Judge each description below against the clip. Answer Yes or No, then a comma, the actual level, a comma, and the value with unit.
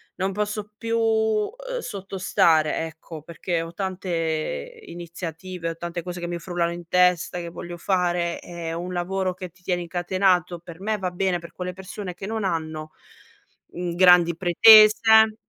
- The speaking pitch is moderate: Yes, medium, 180 Hz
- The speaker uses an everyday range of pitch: No, narrow, 2.3 semitones